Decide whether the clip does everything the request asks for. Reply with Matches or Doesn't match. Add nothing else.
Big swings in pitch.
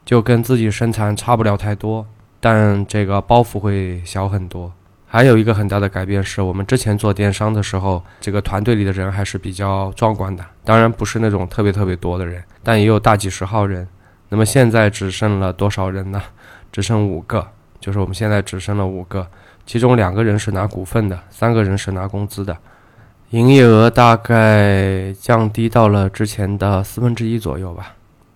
Doesn't match